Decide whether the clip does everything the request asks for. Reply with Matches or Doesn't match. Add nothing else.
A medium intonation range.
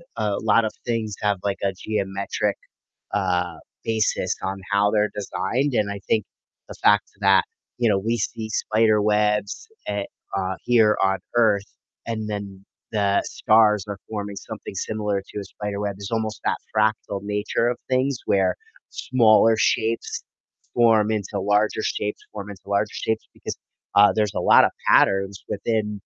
Doesn't match